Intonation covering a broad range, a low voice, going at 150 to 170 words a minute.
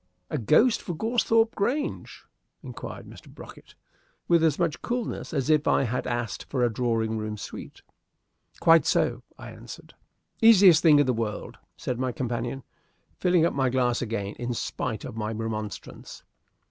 Yes: wide, 6.8 semitones; low, 130 Hz; average, 160 wpm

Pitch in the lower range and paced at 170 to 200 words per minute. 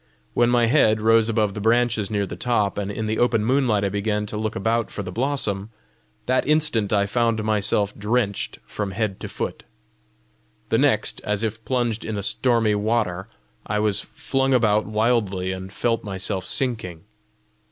Yes: low, 110 Hz; average, 175 wpm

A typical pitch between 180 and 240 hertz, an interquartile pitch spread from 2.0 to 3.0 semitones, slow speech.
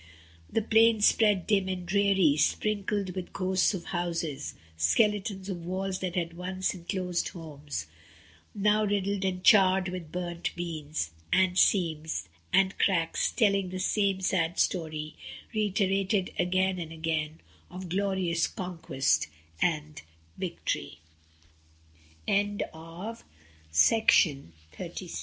Yes: medium, 185 Hz; narrow, 2.6 semitones; slow, 100 wpm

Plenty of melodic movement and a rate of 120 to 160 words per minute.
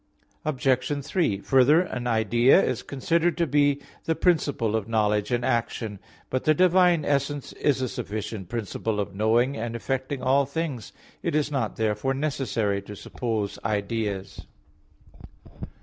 No: average, 4.8 semitones; average, 140 wpm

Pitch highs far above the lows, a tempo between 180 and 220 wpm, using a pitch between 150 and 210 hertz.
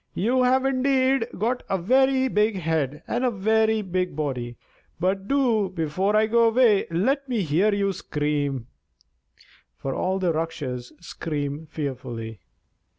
No: wide, 7.7 semitones; slow, 135 wpm; high, 190 Hz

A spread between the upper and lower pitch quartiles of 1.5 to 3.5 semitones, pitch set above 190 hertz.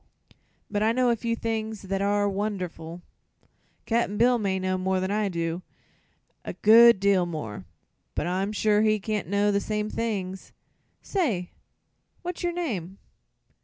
Yes: average, 2.9 semitones; high, 205 Hz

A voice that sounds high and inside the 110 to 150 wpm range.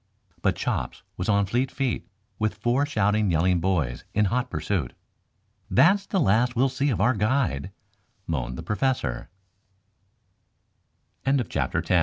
No: low, 110 Hz; slow, 135 wpm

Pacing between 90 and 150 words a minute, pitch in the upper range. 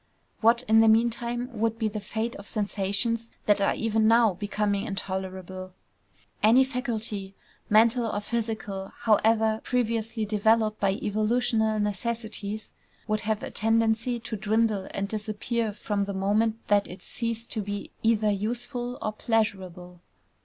Yes: average, 140 wpm; high, 220 Hz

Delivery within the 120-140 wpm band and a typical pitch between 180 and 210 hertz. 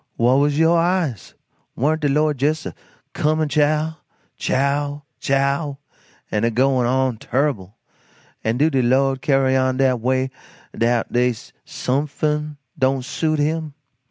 No: slow, 135 wpm; low, 135 Hz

